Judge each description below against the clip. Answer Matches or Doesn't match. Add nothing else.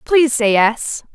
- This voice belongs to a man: Doesn't match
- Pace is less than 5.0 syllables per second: Matches